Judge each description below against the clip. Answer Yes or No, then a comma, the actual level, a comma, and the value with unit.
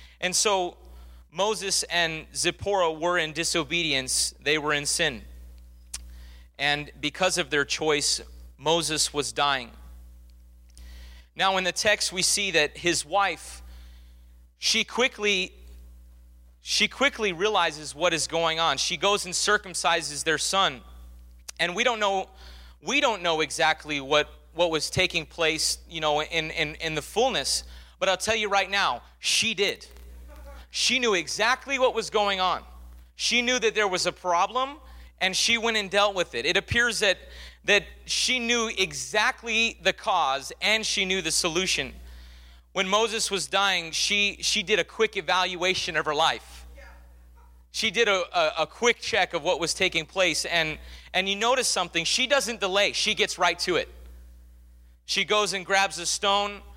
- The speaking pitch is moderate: Yes, medium, 170 Hz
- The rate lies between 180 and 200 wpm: No, average, 160 wpm